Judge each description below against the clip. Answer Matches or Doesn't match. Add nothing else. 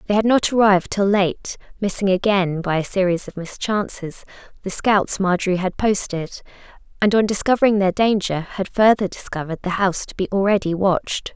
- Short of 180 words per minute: Matches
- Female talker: Matches